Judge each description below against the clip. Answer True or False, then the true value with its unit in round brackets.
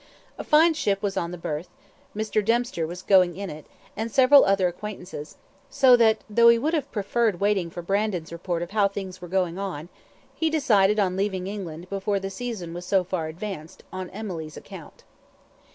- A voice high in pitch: True (195 Hz)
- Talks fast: False (190 wpm)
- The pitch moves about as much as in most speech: True (3.6 semitones)